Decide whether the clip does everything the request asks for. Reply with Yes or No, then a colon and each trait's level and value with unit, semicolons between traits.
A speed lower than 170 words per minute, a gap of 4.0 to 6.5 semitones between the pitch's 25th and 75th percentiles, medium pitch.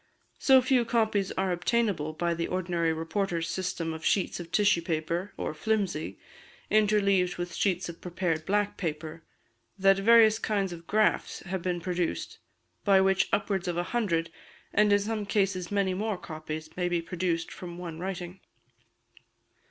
No: average, 155 wpm; average, 3.3 semitones; medium, 180 Hz